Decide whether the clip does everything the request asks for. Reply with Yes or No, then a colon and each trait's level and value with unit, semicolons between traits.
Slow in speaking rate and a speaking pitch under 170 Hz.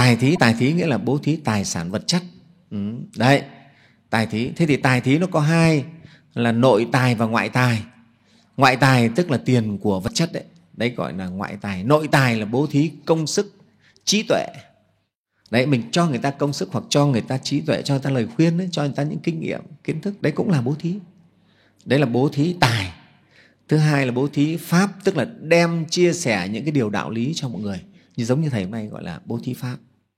No: average, 235 wpm; medium, 140 Hz